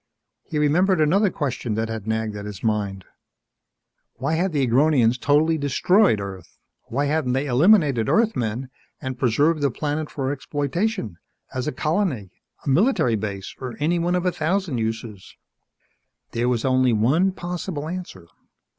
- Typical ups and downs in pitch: No, wide, 6.4 semitones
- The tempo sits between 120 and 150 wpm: Yes, average, 145 wpm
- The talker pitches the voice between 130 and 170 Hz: Yes, medium, 140 Hz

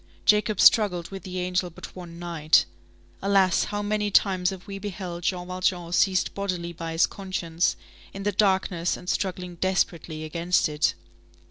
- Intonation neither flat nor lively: No, narrow, 2.2 semitones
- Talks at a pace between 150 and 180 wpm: Yes, average, 155 wpm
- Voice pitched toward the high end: No, medium, 180 Hz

